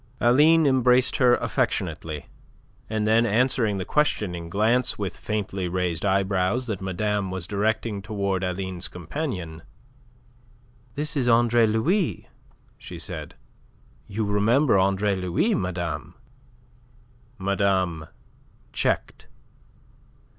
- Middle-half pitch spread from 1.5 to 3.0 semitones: No, average, 4.4 semitones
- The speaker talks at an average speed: No, slow, 100 wpm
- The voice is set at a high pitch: No, low, 105 Hz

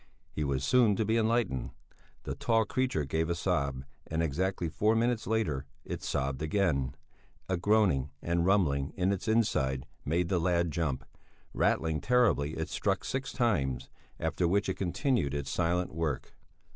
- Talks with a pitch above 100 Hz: No, very low, 85 Hz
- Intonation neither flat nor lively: No, wide, 6.5 semitones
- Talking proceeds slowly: No, average, 160 wpm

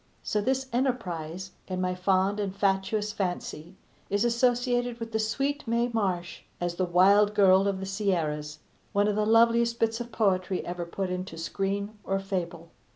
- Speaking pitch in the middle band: No, high, 200 Hz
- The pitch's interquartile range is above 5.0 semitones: No, average, 3.7 semitones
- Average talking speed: Yes, average, 165 wpm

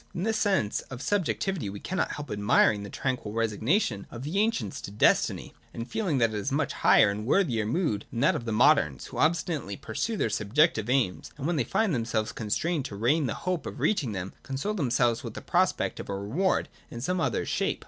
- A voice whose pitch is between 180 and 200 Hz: No, low, 125 Hz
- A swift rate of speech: Yes, fast, 220 wpm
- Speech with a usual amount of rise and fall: No, wide, 8.0 semitones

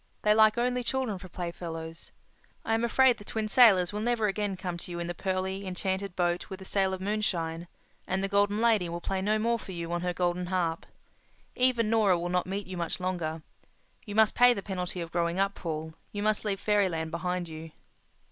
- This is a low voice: No, high, 190 Hz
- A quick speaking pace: Yes, fast, 215 wpm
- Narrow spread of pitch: No, average, 3.5 semitones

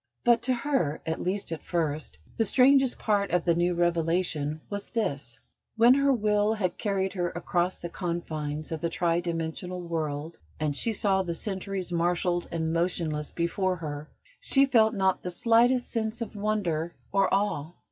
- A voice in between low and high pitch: Yes, medium, 180 Hz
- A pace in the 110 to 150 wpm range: No, average, 165 wpm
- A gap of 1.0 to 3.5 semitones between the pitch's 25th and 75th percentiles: No, average, 4.2 semitones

